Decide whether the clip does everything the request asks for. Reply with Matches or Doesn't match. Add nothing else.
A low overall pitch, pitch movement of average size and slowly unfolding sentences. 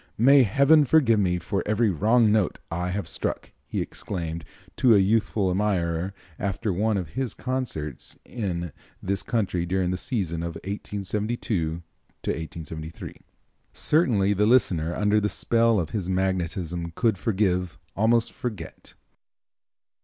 Matches